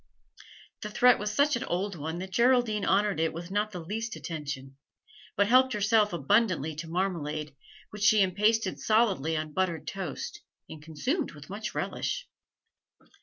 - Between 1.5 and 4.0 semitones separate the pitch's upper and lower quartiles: No, average, 5.2 semitones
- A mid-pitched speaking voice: No, high, 195 Hz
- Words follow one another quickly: No, average, 155 wpm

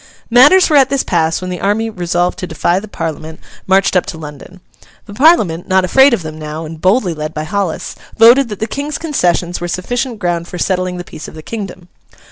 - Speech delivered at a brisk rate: Yes, fast, 215 wpm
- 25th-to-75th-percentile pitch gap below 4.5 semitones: No, average, 5.2 semitones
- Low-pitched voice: No, medium, 185 Hz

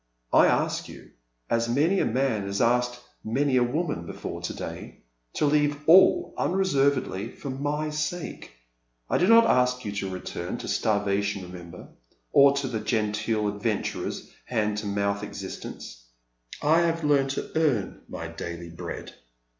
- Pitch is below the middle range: Yes, low, 120 Hz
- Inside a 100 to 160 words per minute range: Yes, average, 155 wpm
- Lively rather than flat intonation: Yes, wide, 6.2 semitones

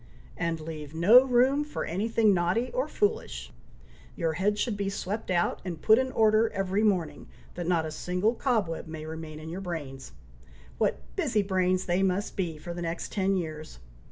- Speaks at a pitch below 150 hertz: No, medium, 185 Hz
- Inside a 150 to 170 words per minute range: No, average, 185 wpm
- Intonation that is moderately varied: Yes, average, 4.6 semitones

